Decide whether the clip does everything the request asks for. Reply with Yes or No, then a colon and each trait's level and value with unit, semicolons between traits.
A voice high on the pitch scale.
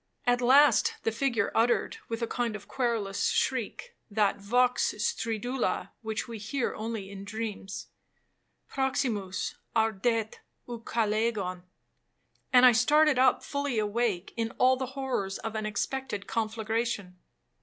Yes: high, 225 Hz